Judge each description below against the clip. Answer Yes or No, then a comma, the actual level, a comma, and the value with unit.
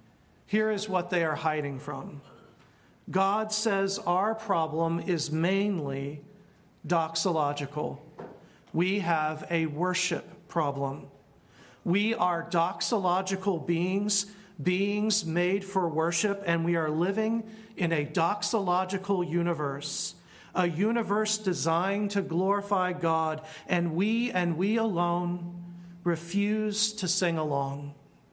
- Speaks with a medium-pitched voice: Yes, medium, 180 Hz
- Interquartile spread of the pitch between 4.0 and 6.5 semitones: No, average, 3.4 semitones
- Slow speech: Yes, slow, 105 wpm